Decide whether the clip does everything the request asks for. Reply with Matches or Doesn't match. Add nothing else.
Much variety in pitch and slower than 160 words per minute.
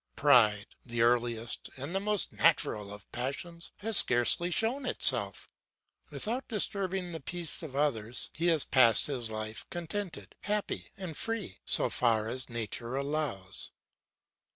Matches